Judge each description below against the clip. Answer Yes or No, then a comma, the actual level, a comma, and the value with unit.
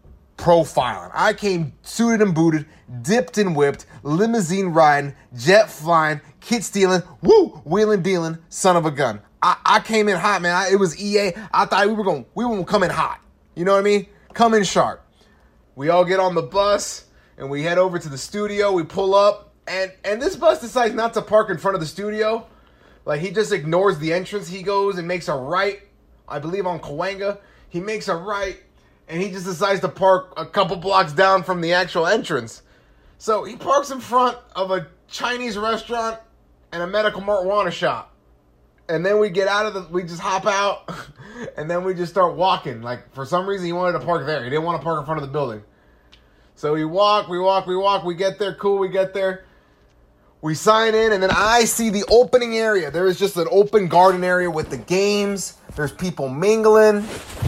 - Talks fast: Yes, fast, 210 wpm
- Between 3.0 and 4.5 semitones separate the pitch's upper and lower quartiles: Yes, average, 4.0 semitones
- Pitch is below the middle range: No, high, 190 Hz